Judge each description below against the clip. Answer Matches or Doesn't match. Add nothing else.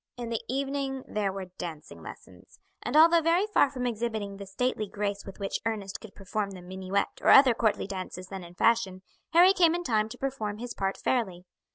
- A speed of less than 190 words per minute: Doesn't match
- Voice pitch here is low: Doesn't match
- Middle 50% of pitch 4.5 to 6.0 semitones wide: Matches